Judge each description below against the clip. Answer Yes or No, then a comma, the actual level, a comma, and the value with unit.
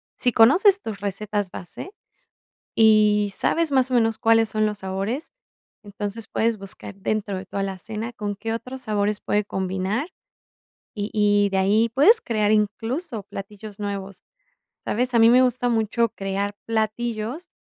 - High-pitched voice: Yes, high, 215 Hz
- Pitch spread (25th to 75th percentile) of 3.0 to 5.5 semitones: No, narrow, 2.4 semitones